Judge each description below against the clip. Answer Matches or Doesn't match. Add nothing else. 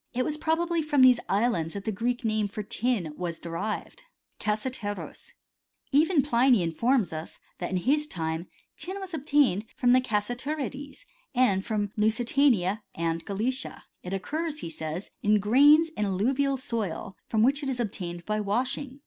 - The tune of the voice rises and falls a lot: Matches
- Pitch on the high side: Matches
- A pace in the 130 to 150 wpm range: Doesn't match